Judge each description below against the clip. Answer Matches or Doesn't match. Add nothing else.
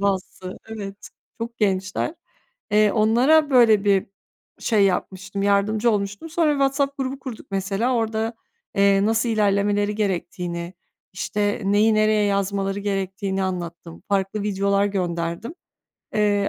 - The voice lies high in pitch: Matches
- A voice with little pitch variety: Matches